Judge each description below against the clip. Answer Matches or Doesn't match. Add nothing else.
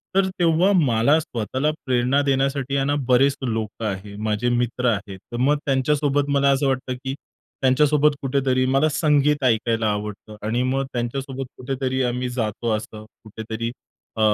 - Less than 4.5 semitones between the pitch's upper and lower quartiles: Matches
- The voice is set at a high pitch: Doesn't match